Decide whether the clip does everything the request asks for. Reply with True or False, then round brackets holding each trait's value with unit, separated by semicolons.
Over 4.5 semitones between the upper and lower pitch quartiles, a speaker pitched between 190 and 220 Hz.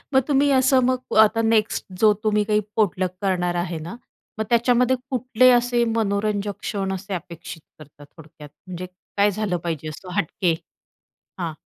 True (5.1 semitones; 205 Hz)